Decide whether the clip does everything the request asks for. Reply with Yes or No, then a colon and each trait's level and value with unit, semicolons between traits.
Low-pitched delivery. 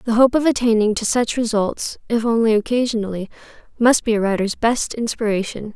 No: high, 225 Hz